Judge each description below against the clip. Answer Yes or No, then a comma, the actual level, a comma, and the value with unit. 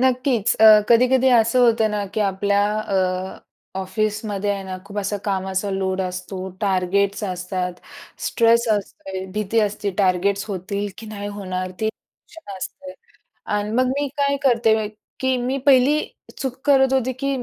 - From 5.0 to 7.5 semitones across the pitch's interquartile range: No, average, 4.3 semitones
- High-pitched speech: Yes, high, 205 Hz